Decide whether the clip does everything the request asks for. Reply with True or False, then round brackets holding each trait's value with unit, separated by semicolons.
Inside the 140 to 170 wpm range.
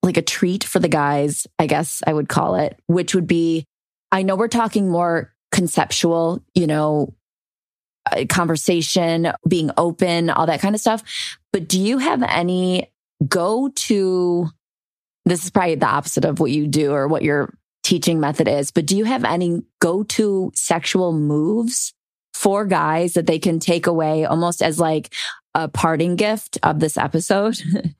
True (165 wpm)